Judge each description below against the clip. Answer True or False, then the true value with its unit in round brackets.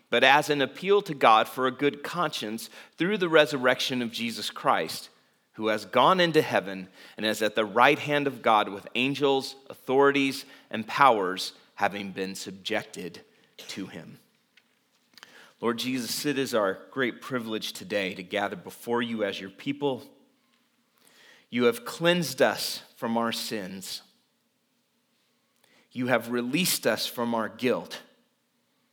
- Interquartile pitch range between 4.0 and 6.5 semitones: True (4.8 semitones)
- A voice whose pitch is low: True (130 Hz)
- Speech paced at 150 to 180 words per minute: False (140 wpm)